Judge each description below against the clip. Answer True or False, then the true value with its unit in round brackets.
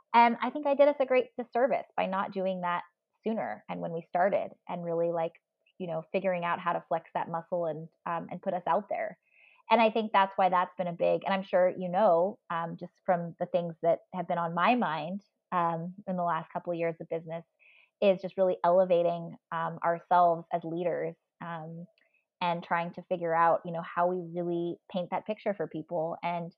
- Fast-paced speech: True (215 wpm)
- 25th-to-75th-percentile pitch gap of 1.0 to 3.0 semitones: True (2.4 semitones)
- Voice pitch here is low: False (175 Hz)